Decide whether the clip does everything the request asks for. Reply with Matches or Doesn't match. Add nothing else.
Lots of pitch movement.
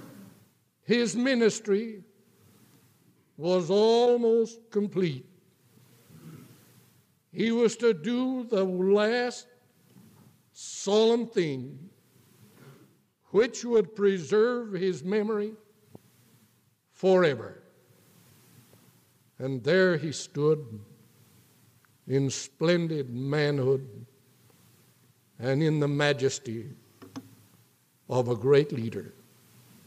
Matches